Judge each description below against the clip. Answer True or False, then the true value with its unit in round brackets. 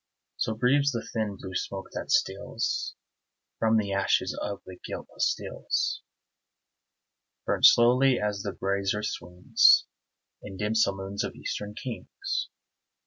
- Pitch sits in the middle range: False (105 Hz)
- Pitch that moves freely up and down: False (2.9 semitones)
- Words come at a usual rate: False (120 wpm)